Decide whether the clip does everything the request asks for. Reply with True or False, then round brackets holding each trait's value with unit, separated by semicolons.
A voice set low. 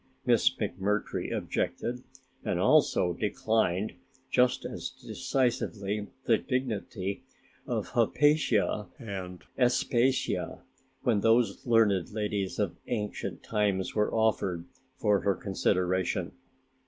True (105 Hz)